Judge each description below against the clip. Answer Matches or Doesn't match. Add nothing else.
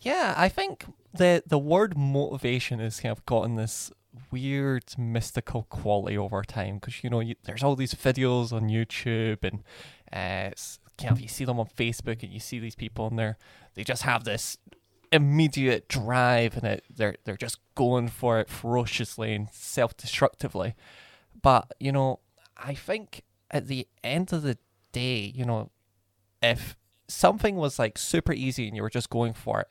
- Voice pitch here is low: Matches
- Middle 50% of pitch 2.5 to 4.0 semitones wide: Matches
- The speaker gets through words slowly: Doesn't match